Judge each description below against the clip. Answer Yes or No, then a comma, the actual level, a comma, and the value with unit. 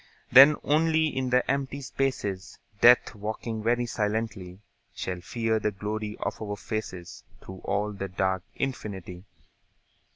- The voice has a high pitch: No, low, 110 Hz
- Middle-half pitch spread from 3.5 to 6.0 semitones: Yes, average, 4.4 semitones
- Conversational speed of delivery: No, slow, 130 wpm